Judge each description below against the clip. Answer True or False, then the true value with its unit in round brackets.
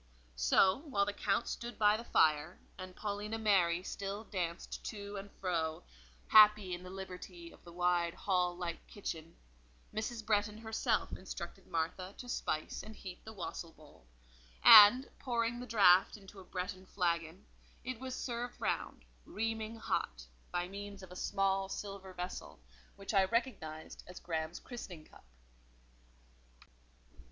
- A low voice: False (190 Hz)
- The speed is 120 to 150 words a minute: True (140 wpm)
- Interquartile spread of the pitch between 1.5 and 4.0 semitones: True (3.7 semitones)